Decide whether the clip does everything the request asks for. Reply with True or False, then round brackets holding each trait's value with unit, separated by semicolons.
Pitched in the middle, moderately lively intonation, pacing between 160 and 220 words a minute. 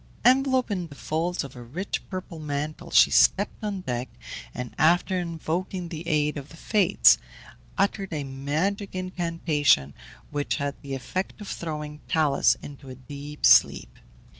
False (160 Hz; 4.4 semitones; 150 wpm)